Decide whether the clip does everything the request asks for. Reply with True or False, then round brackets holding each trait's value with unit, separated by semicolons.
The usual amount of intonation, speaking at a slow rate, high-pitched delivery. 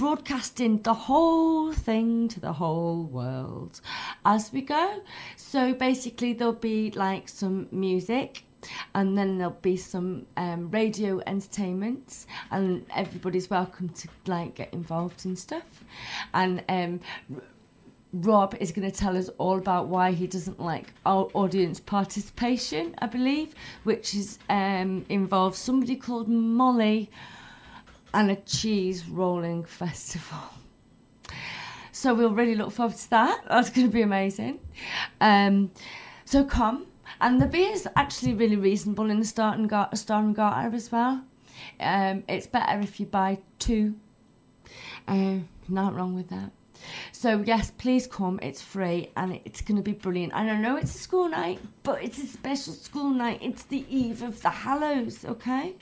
False (4.4 semitones; 155 wpm; 205 Hz)